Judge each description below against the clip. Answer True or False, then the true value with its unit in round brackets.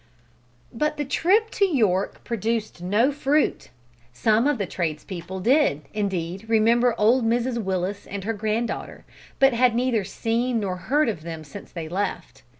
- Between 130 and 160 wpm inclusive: True (150 wpm)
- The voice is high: True (225 Hz)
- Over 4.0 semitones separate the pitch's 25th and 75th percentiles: True (4.8 semitones)